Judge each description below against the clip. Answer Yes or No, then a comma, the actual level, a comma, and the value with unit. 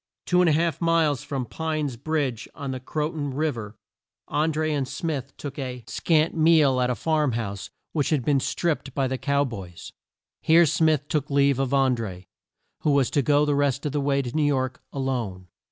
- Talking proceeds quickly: Yes, fast, 210 wpm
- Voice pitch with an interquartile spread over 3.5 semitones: No, average, 3.2 semitones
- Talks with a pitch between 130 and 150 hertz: Yes, medium, 140 Hz